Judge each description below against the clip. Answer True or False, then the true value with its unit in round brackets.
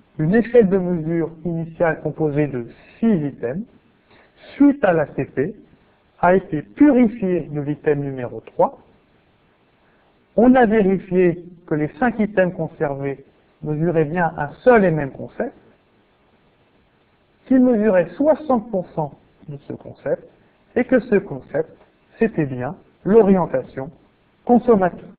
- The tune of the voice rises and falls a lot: True (6.9 semitones)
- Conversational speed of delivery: False (115 wpm)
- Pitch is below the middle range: False (175 Hz)